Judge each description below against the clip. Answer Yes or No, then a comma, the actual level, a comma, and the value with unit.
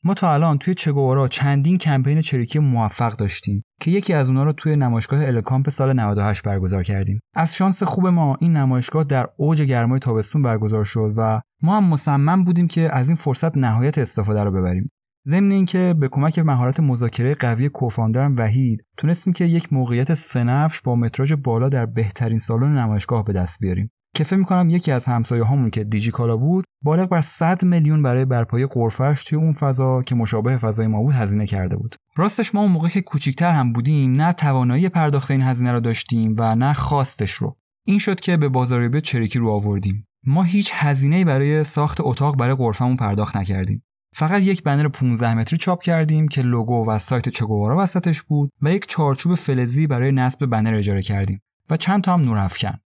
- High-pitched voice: No, low, 135 Hz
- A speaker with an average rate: No, fast, 185 wpm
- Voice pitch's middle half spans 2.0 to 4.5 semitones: No, wide, 5.4 semitones